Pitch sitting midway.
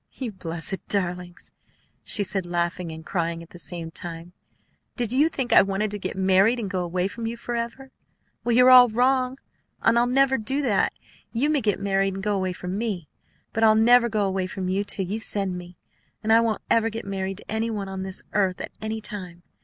No: high, 200 Hz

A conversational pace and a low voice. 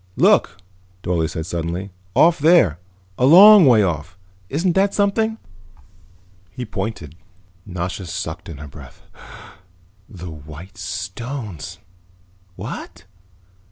No: slow, 105 wpm; very low, 95 Hz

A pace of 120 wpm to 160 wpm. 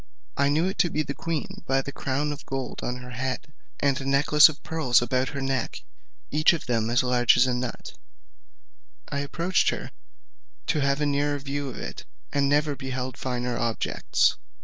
No: average, 195 wpm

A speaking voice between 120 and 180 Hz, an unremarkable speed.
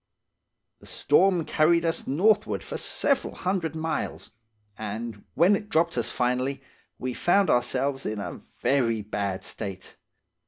No: medium, 140 Hz; slow, 130 wpm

